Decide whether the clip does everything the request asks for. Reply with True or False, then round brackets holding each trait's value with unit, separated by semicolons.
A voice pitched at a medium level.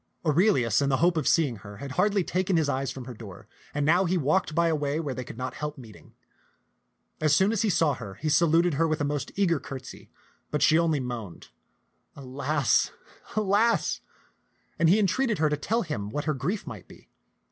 True (150 Hz)